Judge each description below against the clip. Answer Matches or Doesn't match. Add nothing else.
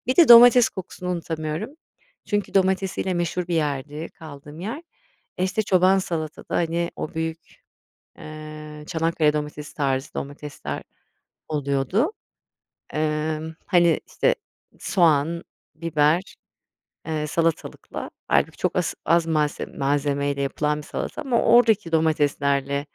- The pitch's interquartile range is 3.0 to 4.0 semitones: Matches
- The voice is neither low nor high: Matches